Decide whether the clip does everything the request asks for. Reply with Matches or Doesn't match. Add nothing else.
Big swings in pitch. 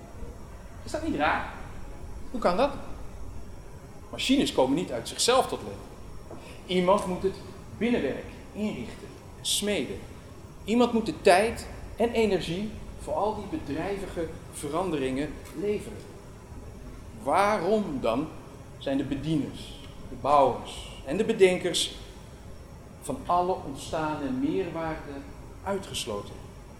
Matches